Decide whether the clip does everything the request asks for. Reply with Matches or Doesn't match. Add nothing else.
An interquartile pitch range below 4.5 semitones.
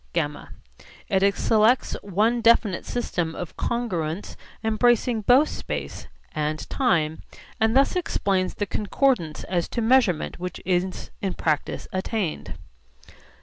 Doesn't match